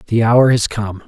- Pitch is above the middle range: No, low, 110 Hz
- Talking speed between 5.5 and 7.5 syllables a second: No, 4.0 syllables/s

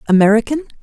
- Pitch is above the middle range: Yes, high, 240 Hz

